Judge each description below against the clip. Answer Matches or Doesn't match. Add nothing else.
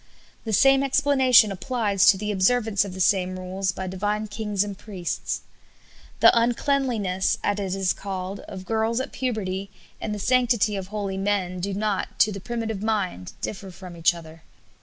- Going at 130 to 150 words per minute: Doesn't match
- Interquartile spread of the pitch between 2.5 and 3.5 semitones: Matches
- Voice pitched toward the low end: Doesn't match